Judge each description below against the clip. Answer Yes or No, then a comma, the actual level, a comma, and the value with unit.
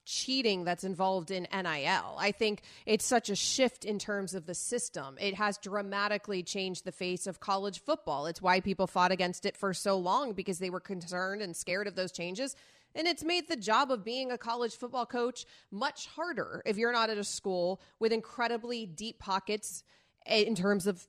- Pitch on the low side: No, high, 205 Hz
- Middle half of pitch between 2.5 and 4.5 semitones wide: Yes, average, 3.8 semitones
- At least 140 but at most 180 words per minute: No, average, 195 wpm